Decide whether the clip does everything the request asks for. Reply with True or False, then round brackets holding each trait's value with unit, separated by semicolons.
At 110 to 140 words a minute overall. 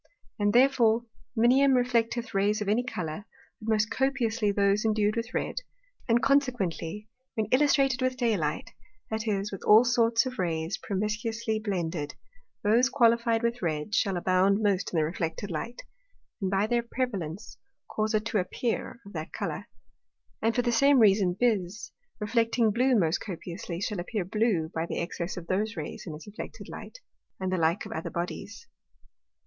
False (165 wpm)